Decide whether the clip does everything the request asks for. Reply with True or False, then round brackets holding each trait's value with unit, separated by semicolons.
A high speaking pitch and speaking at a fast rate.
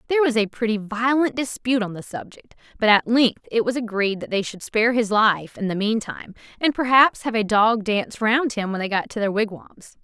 True (225 Hz; 235 wpm)